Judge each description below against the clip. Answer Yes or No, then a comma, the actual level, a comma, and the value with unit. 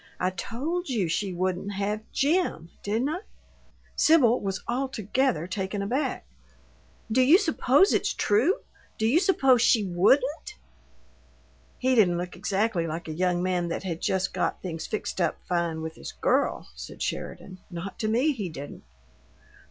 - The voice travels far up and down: Yes, wide, 6.5 semitones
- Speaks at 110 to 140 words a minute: No, average, 150 wpm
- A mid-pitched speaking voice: No, high, 205 Hz